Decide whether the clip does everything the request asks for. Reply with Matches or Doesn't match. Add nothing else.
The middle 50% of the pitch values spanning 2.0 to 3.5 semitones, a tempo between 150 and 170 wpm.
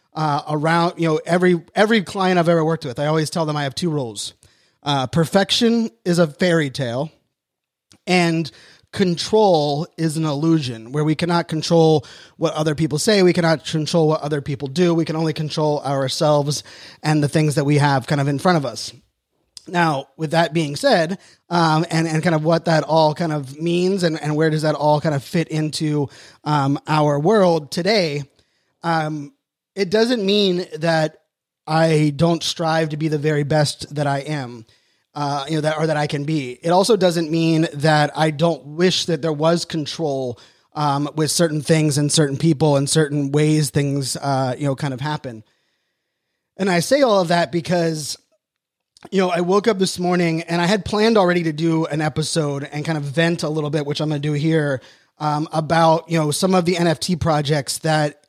Doesn't match